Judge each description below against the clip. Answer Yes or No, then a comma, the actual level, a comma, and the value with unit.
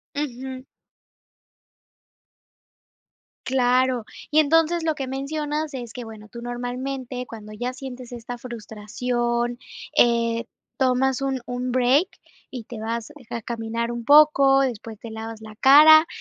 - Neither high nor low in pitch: No, very high, 250 Hz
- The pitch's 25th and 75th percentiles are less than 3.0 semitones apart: Yes, narrow, 2.6 semitones